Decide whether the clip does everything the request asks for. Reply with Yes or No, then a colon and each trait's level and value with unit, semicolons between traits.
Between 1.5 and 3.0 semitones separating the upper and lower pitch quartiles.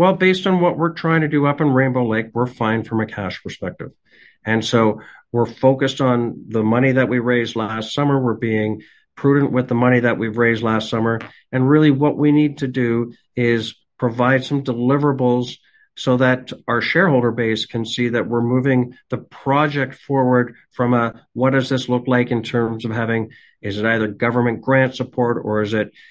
Yes: narrow, 2.6 semitones